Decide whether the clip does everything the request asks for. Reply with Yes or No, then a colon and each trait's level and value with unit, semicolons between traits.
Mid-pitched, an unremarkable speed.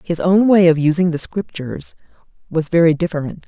Yes: medium, 170 Hz; average, 175 wpm